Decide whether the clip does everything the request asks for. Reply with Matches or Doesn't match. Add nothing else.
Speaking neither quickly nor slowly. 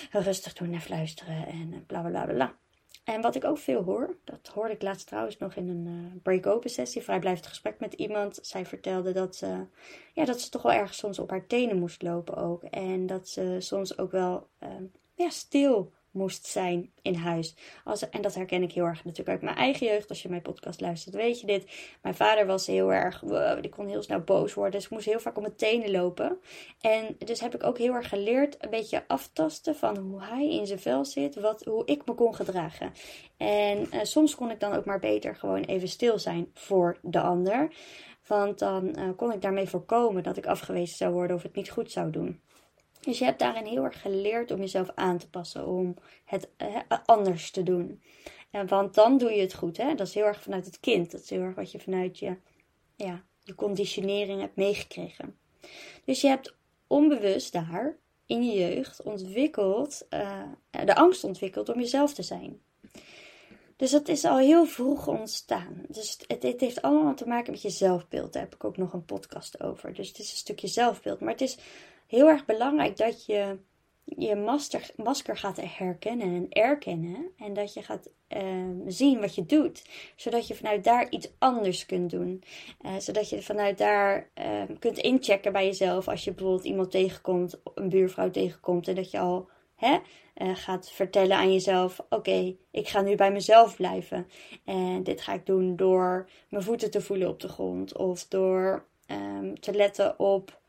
Doesn't match